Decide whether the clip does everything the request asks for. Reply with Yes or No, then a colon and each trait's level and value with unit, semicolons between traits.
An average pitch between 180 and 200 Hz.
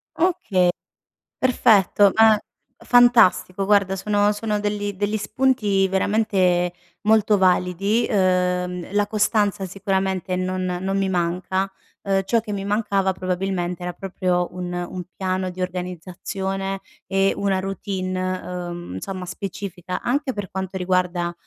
Yes: high, 190 Hz